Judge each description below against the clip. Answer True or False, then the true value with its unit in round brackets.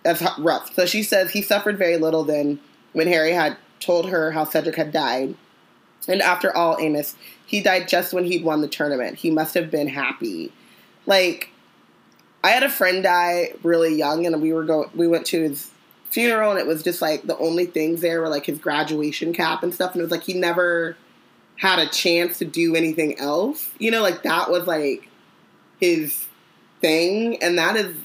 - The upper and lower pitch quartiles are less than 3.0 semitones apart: True (2.6 semitones)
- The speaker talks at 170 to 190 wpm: False (200 wpm)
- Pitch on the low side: False (170 Hz)